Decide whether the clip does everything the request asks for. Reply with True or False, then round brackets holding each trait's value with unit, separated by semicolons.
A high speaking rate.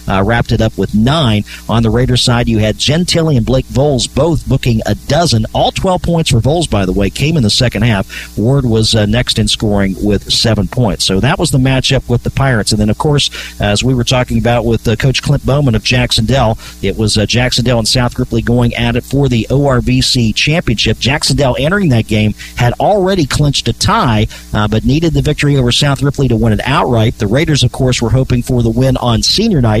True (235 wpm)